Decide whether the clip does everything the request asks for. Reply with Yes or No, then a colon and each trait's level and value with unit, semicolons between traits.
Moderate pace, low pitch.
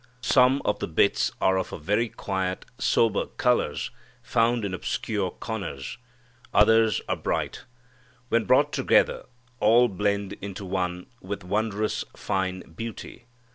No: slow, 125 wpm; low, 100 Hz